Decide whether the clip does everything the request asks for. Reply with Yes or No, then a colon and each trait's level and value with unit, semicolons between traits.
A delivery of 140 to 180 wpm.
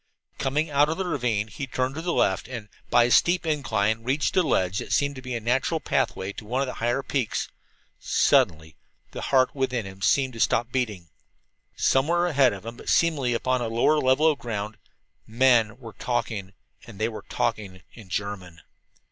No: average, 190 wpm